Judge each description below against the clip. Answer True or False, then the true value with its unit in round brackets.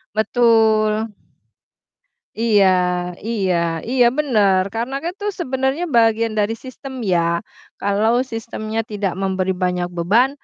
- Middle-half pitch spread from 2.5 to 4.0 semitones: True (3.2 semitones)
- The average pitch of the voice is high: True (220 Hz)